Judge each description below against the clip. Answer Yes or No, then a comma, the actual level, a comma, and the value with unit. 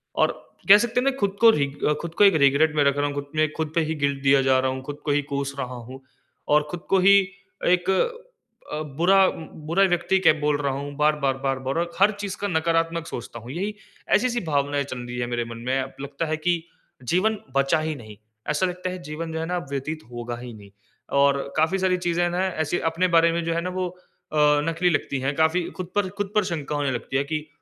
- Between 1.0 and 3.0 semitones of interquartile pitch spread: No, average, 4.2 semitones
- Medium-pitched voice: Yes, medium, 155 Hz